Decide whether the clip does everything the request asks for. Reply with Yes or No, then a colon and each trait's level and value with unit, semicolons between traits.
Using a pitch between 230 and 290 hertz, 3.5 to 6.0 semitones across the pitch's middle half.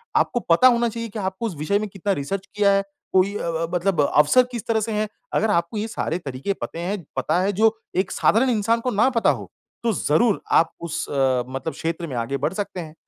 No: high, 195 Hz; average, 5.2 semitones